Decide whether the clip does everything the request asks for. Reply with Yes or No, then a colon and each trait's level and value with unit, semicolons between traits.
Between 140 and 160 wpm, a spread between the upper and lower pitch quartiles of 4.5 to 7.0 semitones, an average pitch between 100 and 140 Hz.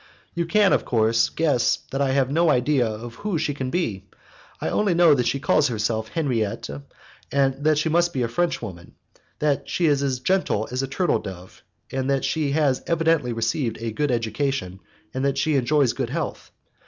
No: average, 180 wpm; average, 4.9 semitones; low, 135 Hz